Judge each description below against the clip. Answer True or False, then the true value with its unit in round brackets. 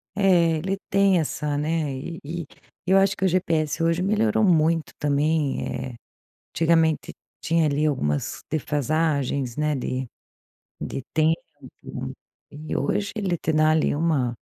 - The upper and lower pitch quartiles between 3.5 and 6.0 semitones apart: False (2.9 semitones)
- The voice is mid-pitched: True (160 Hz)